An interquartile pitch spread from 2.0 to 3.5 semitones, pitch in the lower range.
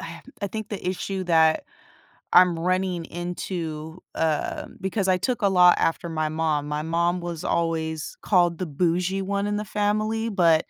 No: average, 2.8 semitones; medium, 175 Hz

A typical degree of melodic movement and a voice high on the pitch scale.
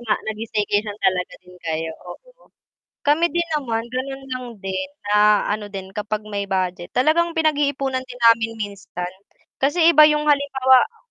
No: wide, 6.1 semitones; high, 230 Hz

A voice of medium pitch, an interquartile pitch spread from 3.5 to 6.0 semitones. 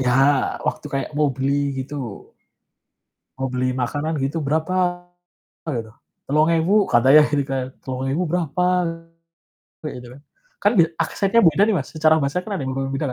Yes: medium, 145 Hz; average, 3.8 semitones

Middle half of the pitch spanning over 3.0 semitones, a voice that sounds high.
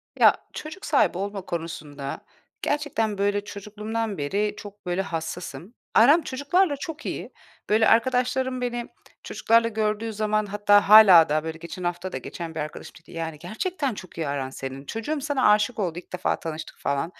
Yes: wide, 5.4 semitones; high, 205 Hz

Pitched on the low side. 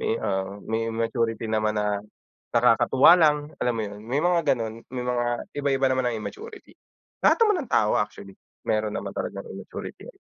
Yes: low, 115 Hz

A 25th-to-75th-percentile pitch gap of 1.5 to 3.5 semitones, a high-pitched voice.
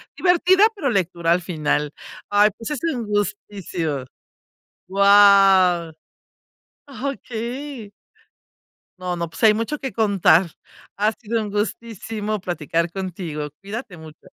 No: average, 4.7 semitones; high, 200 Hz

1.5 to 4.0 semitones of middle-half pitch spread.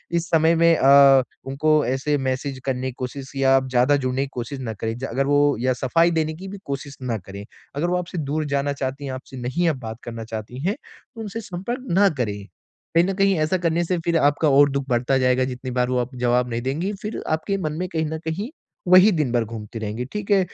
No: average, 4.9 semitones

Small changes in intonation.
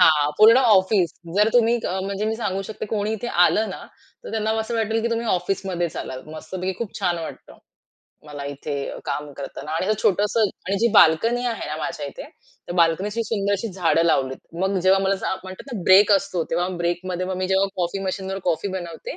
No: average, 3.7 semitones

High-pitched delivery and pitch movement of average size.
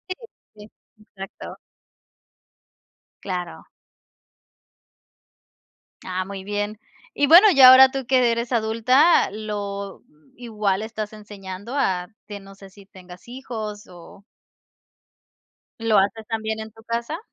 Yes: high, 215 Hz; average, 3.1 semitones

